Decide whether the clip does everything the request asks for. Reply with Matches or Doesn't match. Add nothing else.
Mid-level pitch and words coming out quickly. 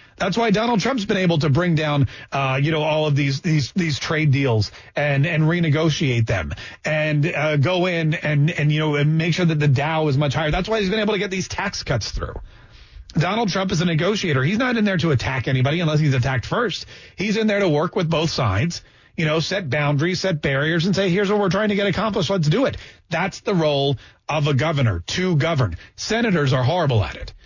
Matches